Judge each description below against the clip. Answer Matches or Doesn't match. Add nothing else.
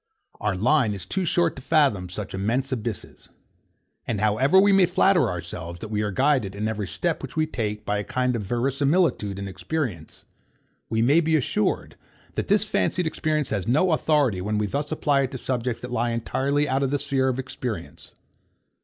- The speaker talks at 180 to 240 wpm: Matches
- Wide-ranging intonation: Matches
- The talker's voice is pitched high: Doesn't match